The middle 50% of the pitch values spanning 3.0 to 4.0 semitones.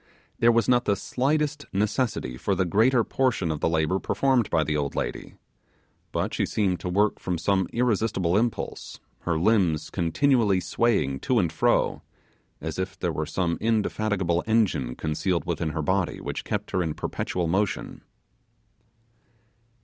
No: average, 5.2 semitones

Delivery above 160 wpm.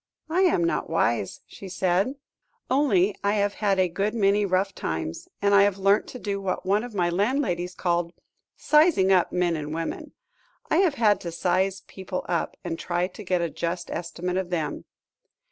Yes: average, 185 wpm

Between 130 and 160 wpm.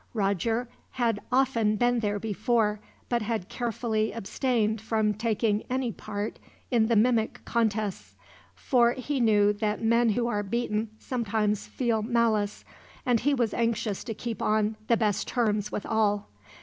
Yes: average, 150 wpm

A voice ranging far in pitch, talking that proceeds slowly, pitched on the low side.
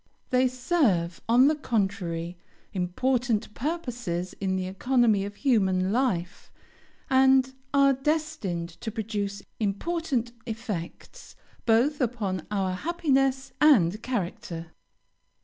No: wide, 5.9 semitones; slow, 100 wpm; high, 225 Hz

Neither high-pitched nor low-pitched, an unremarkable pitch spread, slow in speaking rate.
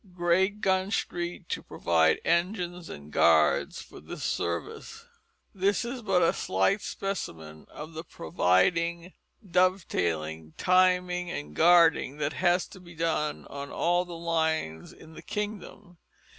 Yes: medium, 170 Hz; average, 4.7 semitones; slow, 130 wpm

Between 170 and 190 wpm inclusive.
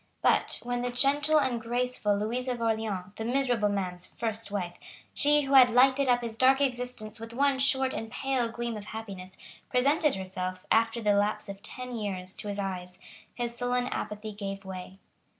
Yes: average, 180 wpm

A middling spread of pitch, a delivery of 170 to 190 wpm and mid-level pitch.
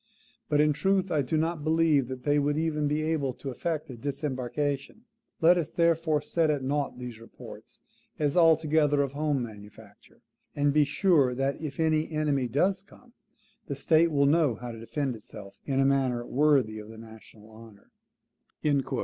Yes: average, 3.8 semitones; average, 175 wpm; medium, 145 Hz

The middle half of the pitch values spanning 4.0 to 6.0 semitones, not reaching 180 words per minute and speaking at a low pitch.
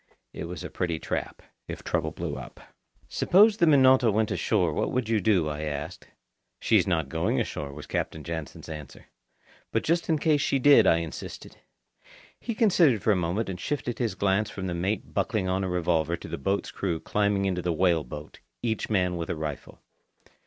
No: wide, 5.4 semitones; average, 190 wpm; very low, 95 Hz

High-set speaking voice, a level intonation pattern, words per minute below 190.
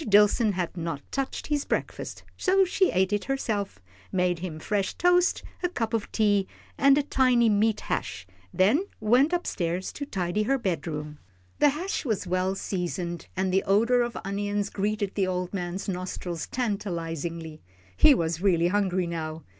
No: high, 200 Hz; average, 5.1 semitones; average, 160 wpm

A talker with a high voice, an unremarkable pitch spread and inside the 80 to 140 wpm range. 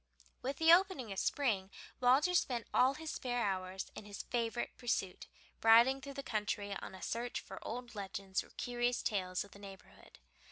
No: high, 235 Hz; average, 4.7 semitones; average, 175 wpm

